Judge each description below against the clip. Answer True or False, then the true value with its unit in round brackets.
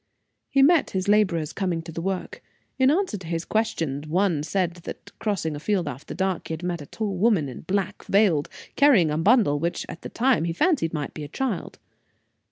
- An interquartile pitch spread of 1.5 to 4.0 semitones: False (4.7 semitones)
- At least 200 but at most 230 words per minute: True (205 wpm)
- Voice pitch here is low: False (180 Hz)